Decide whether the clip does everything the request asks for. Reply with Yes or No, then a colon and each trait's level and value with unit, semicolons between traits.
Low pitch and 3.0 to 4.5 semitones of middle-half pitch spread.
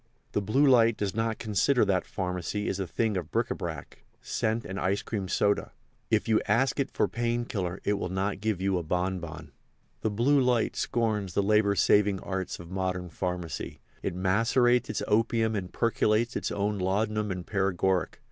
Yes: low, 100 Hz; average, 3.3 semitones